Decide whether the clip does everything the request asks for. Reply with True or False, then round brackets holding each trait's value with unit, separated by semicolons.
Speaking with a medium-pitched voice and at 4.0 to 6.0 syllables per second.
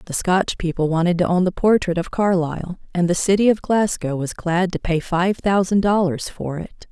True (180 Hz; 5.0 syllables/s)